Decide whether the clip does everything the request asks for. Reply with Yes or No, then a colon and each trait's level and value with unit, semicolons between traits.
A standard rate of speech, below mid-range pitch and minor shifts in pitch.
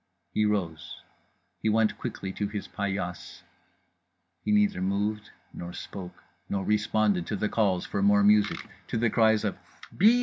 Yes: average, 155 wpm; low, 105 Hz; narrow, 1.8 semitones